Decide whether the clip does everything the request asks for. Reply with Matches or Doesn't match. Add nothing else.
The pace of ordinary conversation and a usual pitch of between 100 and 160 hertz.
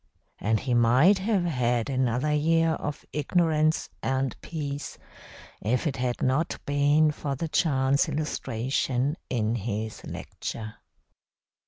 Doesn't match